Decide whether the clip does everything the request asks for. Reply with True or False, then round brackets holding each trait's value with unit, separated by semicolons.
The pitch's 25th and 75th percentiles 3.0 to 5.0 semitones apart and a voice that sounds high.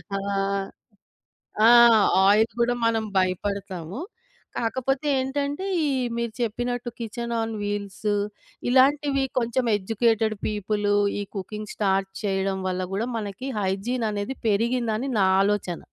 True (3.5 semitones; 220 Hz)